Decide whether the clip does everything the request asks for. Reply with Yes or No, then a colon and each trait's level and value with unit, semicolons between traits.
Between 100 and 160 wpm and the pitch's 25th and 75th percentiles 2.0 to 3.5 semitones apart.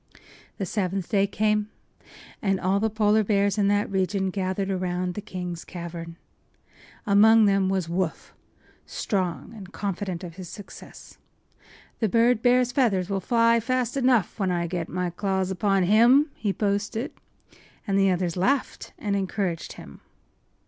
Yes: average, 150 wpm; average, 2.9 semitones